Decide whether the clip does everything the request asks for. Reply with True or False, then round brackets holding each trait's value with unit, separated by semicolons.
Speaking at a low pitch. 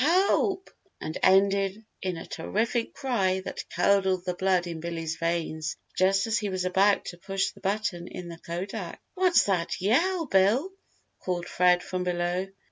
False (190 Hz)